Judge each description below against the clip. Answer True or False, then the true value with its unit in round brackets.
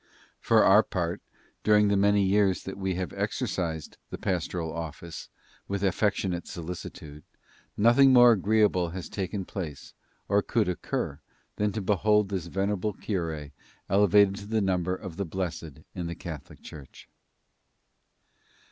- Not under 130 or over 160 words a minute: True (140 wpm)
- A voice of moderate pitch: False (95 Hz)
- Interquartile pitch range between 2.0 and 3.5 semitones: True (3.2 semitones)